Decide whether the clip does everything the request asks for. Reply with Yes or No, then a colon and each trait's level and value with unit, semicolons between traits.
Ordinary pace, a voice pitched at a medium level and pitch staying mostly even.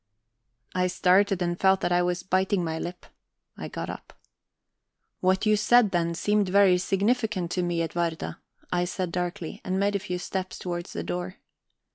Yes: average, 170 wpm; medium, 180 Hz; narrow, 2.0 semitones